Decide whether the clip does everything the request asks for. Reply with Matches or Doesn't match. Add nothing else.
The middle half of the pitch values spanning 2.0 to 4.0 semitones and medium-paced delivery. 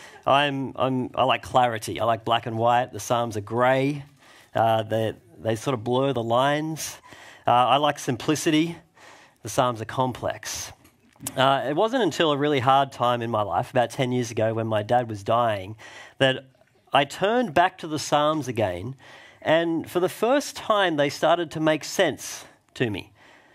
Doesn't match